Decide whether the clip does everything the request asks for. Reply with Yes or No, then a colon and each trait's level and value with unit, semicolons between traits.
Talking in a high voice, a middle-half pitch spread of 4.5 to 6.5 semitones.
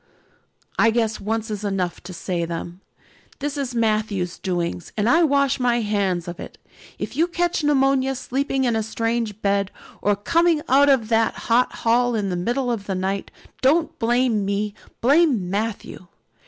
Yes: high, 225 Hz; average, 5.0 semitones